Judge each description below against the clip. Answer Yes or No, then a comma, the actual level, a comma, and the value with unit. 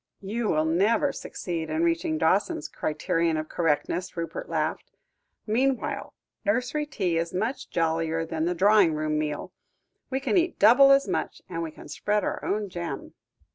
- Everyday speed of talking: Yes, average, 160 wpm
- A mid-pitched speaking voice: Yes, medium, 175 Hz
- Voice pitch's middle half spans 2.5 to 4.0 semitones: No, average, 5.2 semitones